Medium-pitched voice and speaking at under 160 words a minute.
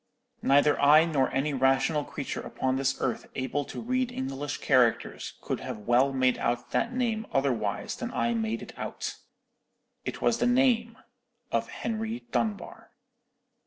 Yes: medium, 145 Hz; average, 150 wpm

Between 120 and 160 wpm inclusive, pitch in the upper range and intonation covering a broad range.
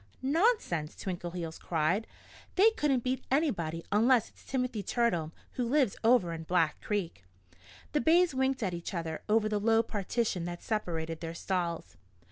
Yes: average, 150 wpm; high, 205 Hz; wide, 6.9 semitones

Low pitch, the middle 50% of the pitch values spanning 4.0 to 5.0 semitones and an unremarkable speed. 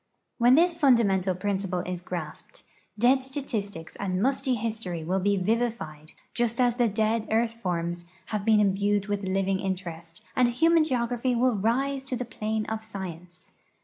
No: high, 215 Hz; average, 4.4 semitones; average, 160 wpm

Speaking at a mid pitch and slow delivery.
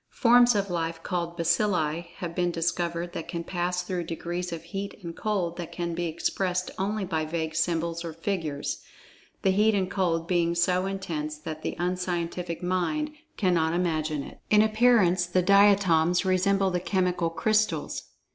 No: medium, 175 Hz; average, 160 wpm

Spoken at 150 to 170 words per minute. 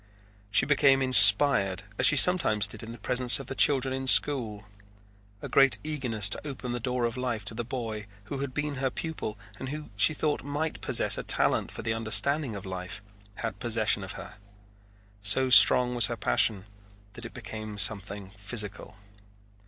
No: average, 180 wpm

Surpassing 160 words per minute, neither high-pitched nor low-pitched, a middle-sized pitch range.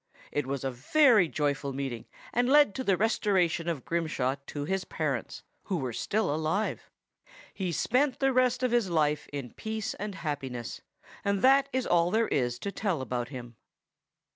No: average, 170 wpm; medium, 170 Hz; wide, 7.9 semitones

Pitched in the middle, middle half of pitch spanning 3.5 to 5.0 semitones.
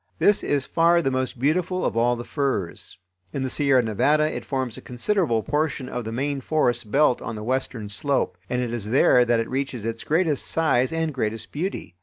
No: low, 130 Hz; average, 4.2 semitones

